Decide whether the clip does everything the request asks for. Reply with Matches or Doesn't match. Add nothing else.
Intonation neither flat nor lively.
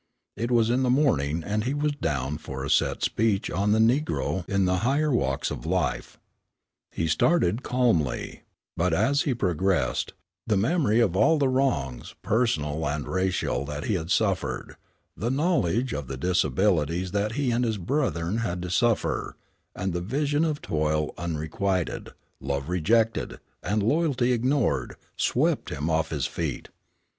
Doesn't match